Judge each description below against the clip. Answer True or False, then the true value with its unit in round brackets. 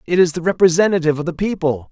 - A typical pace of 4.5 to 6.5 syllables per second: False (7.3 syllables/s)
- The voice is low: False (170 Hz)